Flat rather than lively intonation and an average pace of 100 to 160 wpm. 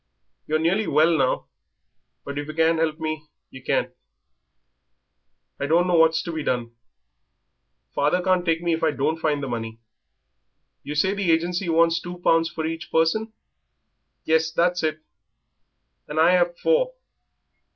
Yes: narrow, 2.1 semitones; average, 150 wpm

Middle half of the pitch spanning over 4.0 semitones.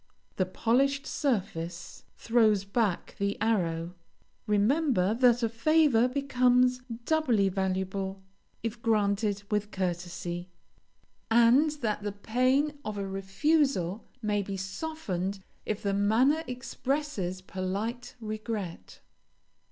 Yes: average, 4.5 semitones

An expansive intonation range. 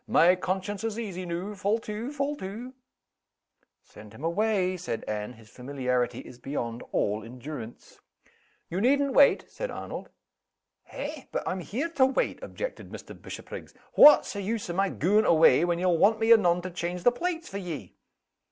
Yes: wide, 6.4 semitones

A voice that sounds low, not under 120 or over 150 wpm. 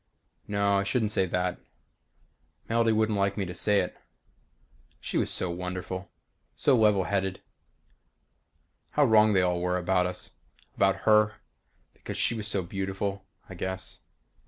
Yes: very low, 95 Hz; average, 145 wpm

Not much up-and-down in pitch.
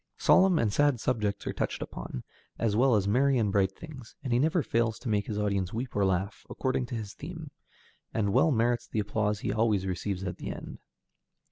No: average, 4.3 semitones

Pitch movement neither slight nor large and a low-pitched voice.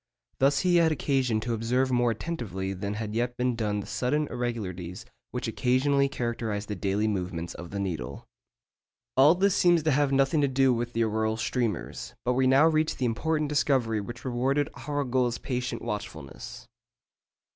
Yes: average, 4.2 semitones; low, 120 Hz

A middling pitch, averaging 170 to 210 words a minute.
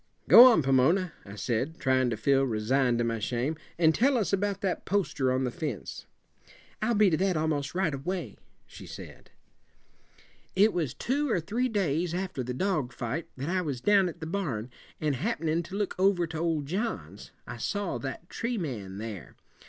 Yes: medium, 160 Hz; average, 185 wpm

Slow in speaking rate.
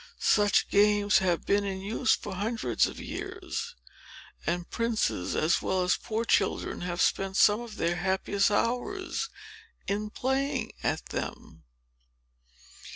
Yes: slow, 130 wpm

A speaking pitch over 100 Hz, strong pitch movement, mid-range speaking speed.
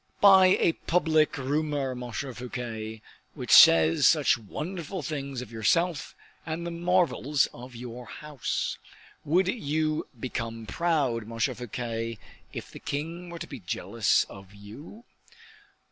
No: medium, 140 Hz; wide, 6.1 semitones; slow, 130 wpm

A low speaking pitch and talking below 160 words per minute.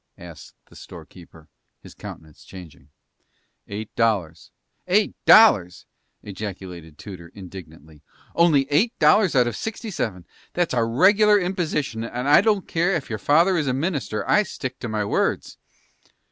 Yes: low, 120 Hz; average, 145 wpm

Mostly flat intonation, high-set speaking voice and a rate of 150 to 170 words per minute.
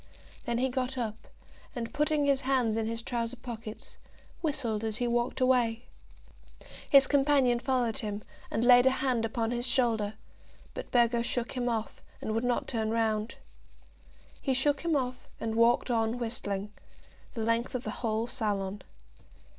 Yes: narrow, 2.3 semitones; high, 240 Hz; average, 160 wpm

